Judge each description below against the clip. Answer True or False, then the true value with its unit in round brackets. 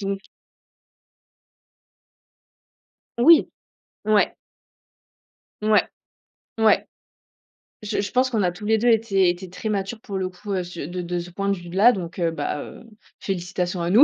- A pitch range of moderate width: True (3.3 semitones)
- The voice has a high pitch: True (195 Hz)